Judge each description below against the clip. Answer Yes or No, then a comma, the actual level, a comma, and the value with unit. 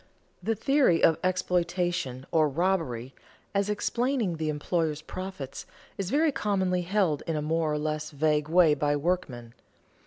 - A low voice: No, medium, 165 Hz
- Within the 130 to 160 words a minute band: Yes, average, 145 wpm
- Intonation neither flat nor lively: Yes, average, 3.9 semitones